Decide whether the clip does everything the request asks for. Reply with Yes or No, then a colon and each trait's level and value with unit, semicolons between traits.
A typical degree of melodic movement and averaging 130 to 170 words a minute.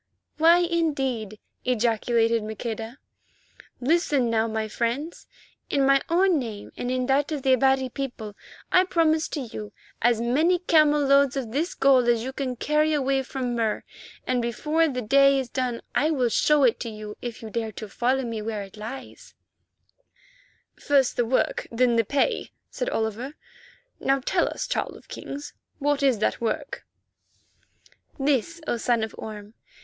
Yes: average, 3.9 semitones; average, 165 wpm